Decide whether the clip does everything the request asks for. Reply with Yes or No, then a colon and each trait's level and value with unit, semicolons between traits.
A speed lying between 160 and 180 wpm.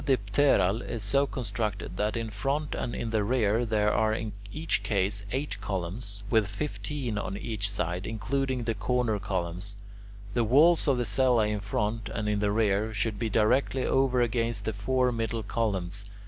Yes: average, 175 wpm